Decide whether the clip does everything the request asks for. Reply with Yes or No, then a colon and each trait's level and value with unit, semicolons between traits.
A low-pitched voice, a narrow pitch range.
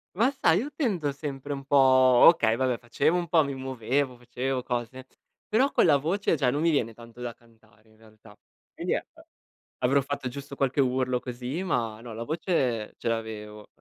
No: low, 130 Hz; average, 3.7 semitones